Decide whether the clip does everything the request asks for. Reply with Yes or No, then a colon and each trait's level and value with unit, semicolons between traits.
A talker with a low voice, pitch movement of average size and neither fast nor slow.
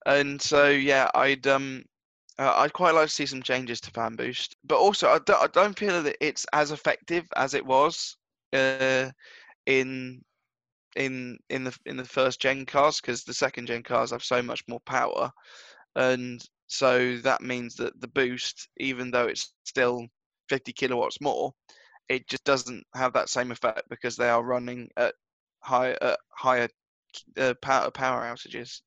No: low, 130 Hz; narrow, 1.8 semitones; average, 175 wpm